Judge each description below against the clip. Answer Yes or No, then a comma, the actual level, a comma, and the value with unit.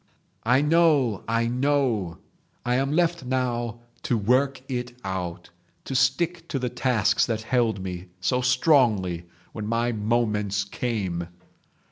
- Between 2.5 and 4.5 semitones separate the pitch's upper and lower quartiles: Yes, average, 3.9 semitones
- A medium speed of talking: No, slow, 130 wpm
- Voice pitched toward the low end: Yes, low, 120 Hz